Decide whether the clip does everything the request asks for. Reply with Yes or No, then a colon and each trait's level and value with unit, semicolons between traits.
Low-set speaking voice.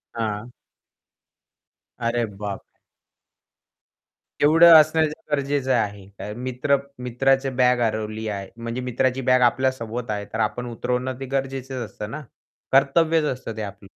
Yes: low, 125 Hz